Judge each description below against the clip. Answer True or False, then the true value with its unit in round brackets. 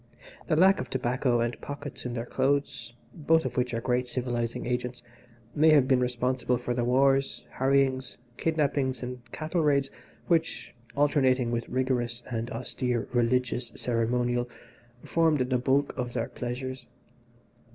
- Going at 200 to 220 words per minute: False (140 wpm)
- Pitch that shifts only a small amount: True (2.2 semitones)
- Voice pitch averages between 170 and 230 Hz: False (125 Hz)